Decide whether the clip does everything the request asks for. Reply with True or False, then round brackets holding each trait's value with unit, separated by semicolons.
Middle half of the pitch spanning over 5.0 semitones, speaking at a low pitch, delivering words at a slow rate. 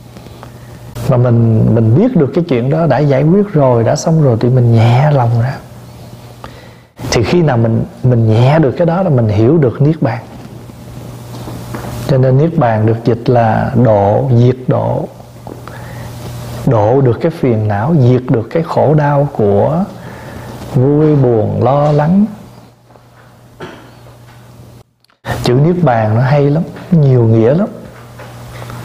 False (4.0 semitones; 125 Hz; 145 wpm)